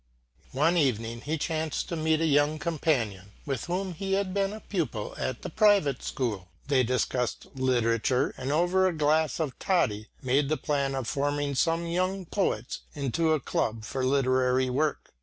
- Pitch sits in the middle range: Yes, medium, 145 Hz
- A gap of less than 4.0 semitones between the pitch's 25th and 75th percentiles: No, average, 4.5 semitones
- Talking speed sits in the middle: Yes, average, 170 wpm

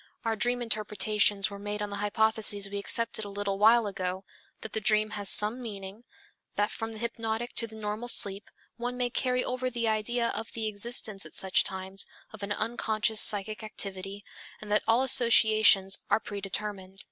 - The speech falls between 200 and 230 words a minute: No, average, 180 wpm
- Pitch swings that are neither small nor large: No, narrow, 2.2 semitones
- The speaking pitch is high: Yes, high, 215 Hz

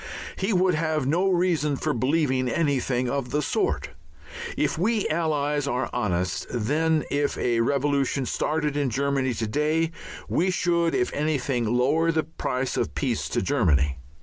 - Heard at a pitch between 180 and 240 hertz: No, medium, 145 Hz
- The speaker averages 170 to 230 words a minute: No, average, 150 wpm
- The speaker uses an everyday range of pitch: Yes, average, 4.3 semitones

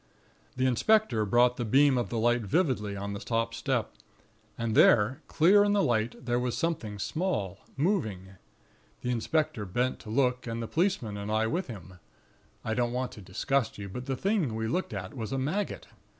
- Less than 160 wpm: No, average, 190 wpm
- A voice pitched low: Yes, low, 120 Hz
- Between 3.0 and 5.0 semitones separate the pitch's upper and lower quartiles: Yes, average, 4.4 semitones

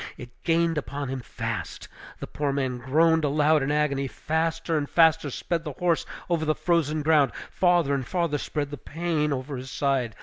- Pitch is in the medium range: Yes, medium, 150 Hz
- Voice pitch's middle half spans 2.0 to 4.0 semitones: Yes, average, 2.8 semitones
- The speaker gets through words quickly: No, average, 180 wpm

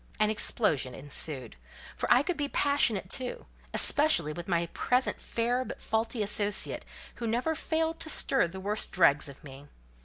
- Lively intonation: Yes, wide, 7.7 semitones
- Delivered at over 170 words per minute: No, average, 160 wpm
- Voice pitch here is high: Yes, high, 215 Hz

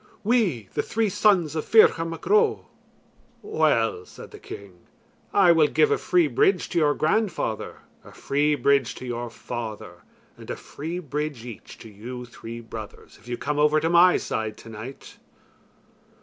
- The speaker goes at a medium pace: Yes, average, 165 wpm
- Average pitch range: No, wide, 7.2 semitones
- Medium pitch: Yes, medium, 150 Hz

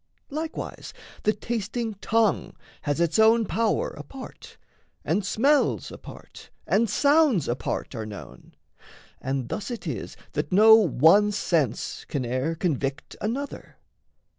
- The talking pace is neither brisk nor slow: No, slow, 120 wpm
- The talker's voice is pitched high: Yes, high, 205 Hz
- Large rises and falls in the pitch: Yes, wide, 7.9 semitones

